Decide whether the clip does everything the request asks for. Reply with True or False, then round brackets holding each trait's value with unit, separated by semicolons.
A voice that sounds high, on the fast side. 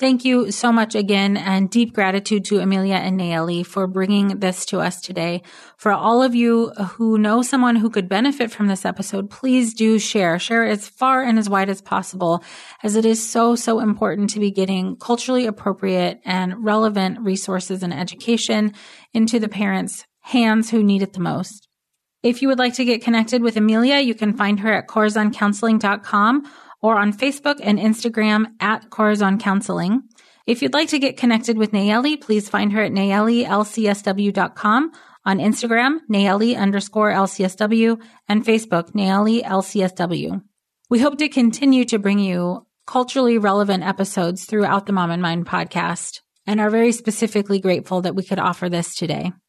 False (210 Hz; 170 wpm)